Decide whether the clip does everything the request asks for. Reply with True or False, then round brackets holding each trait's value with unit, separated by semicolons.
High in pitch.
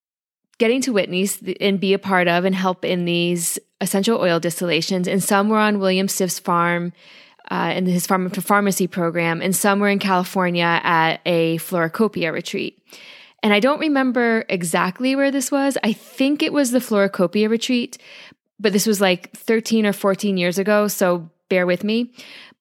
True (195 Hz)